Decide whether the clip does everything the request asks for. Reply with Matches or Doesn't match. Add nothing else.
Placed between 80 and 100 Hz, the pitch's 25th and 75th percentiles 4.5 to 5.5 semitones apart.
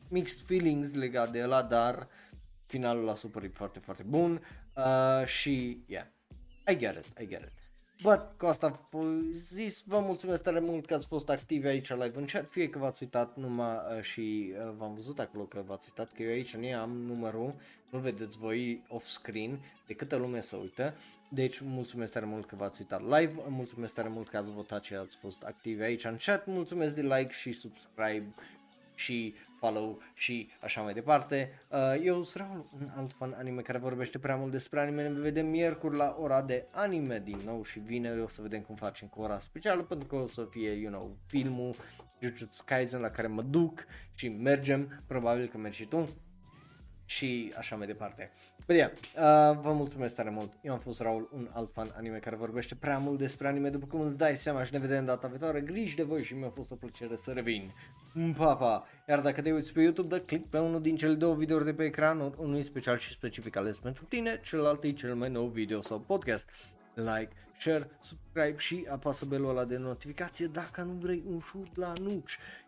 Doesn't match